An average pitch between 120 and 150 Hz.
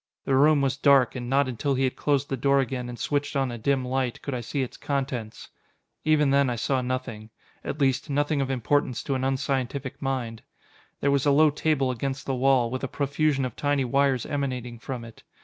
Yes: low, 135 Hz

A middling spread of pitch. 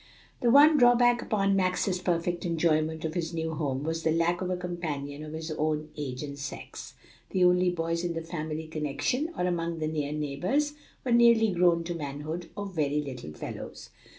Yes: average, 3.1 semitones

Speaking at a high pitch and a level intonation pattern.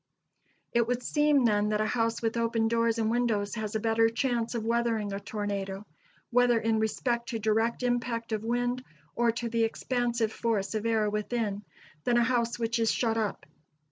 Yes: high, 230 Hz; narrow, 1.6 semitones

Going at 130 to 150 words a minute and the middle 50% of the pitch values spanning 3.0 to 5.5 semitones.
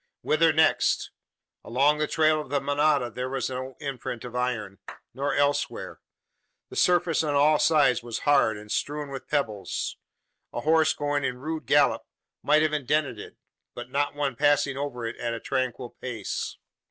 No: average, 165 wpm; average, 3.3 semitones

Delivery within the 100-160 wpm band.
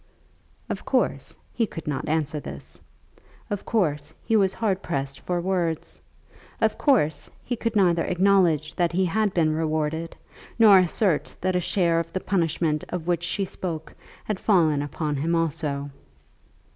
Yes: average, 155 wpm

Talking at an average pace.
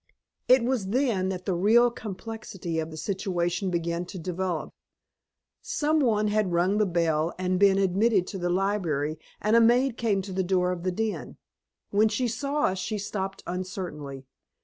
Yes: average, 170 wpm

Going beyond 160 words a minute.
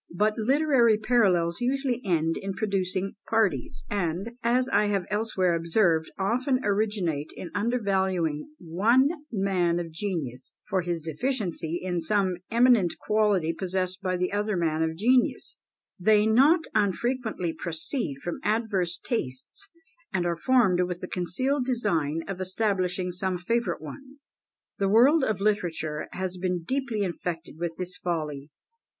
No: slow, 135 wpm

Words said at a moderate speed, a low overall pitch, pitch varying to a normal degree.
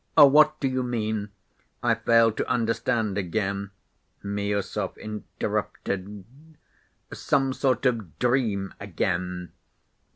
No: slow, 95 wpm; low, 110 Hz; average, 3.7 semitones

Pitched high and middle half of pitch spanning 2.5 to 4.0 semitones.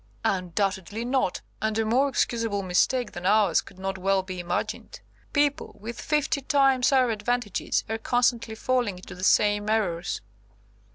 No: high, 220 Hz; average, 4.5 semitones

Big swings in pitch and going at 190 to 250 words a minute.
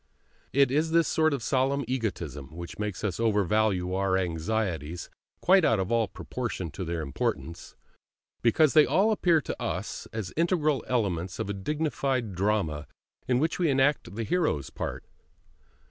No: wide, 7.7 semitones; average, 155 wpm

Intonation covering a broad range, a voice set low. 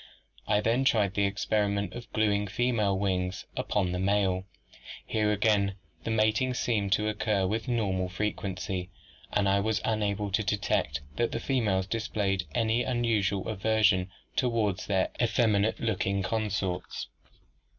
No: narrow, 2.4 semitones; low, 105 Hz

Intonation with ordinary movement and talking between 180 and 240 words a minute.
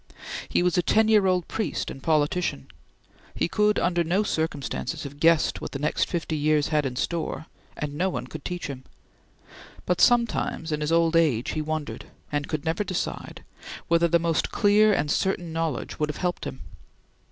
Yes: average, 3.0 semitones; average, 185 wpm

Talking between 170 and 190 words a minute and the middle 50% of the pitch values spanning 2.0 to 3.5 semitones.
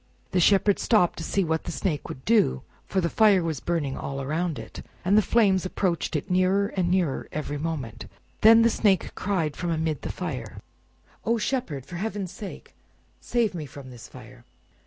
No: average, 185 wpm; average, 4.9 semitones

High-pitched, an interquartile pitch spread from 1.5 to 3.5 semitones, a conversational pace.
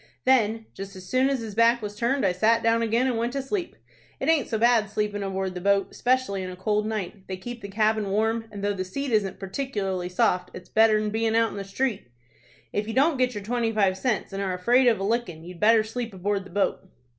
No: high, 215 Hz; average, 3.2 semitones; fast, 240 wpm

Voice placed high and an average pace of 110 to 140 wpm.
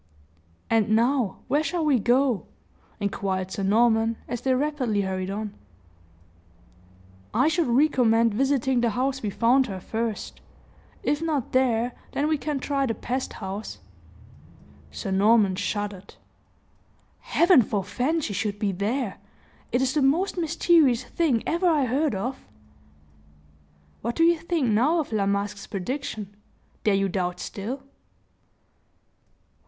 Yes: high, 240 Hz; slow, 135 wpm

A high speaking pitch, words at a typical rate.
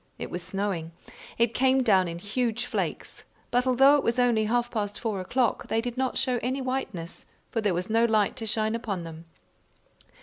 Yes: high, 225 Hz; average, 195 wpm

